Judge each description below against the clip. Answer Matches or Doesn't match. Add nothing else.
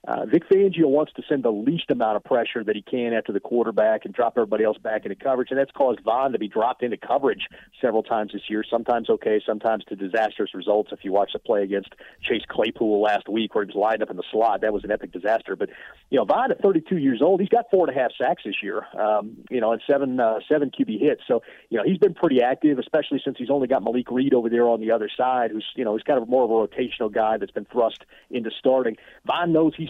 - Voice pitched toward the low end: Matches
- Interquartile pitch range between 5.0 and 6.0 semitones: Matches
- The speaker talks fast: Matches